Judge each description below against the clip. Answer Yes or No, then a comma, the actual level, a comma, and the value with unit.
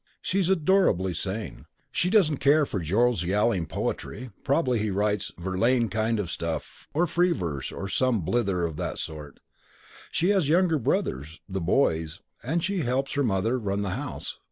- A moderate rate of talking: Yes, average, 165 wpm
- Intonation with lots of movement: Yes, wide, 7.8 semitones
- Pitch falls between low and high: No, low, 110 Hz